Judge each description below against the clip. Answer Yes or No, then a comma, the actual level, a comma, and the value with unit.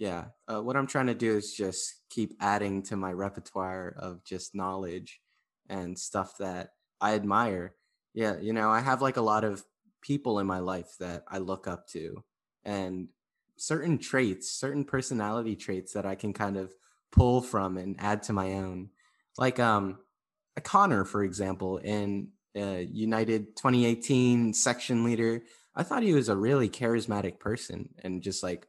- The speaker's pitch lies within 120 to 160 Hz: No, low, 105 Hz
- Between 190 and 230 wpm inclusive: No, average, 170 wpm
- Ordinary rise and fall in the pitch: Yes, average, 3.7 semitones